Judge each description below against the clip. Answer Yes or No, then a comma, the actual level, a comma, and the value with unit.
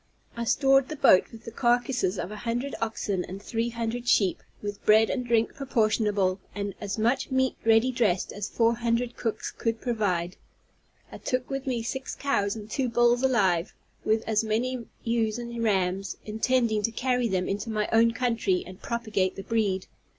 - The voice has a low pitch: No, high, 225 Hz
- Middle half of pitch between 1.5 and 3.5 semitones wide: Yes, average, 2.8 semitones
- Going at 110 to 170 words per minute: No, average, 180 wpm